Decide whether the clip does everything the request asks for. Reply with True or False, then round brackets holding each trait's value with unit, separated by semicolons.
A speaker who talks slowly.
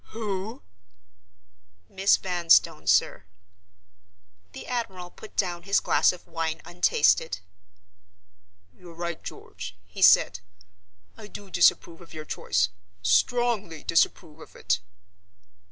True (105 wpm)